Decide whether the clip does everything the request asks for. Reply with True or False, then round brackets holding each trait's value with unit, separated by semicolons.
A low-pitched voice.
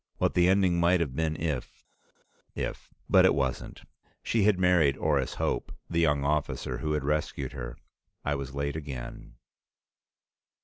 True (75 Hz)